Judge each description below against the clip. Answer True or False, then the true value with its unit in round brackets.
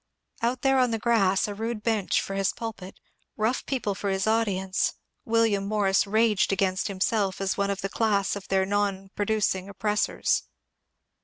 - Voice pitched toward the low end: False (205 Hz)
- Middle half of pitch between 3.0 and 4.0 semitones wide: False (2.4 semitones)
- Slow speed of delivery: False (170 wpm)